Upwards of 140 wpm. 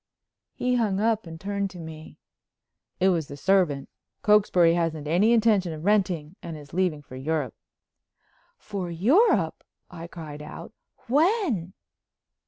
No: slow, 135 wpm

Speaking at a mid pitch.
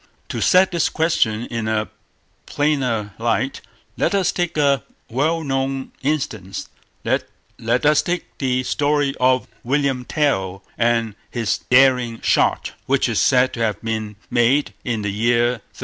No: low, 125 Hz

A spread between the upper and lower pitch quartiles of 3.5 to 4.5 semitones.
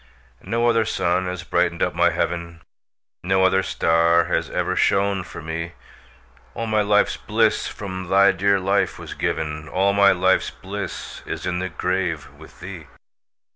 No: narrow, 2.6 semitones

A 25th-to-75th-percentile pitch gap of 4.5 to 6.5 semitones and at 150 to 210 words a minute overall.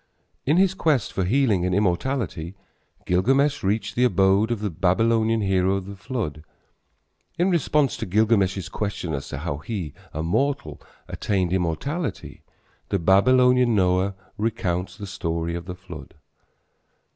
No: average, 4.8 semitones; average, 140 wpm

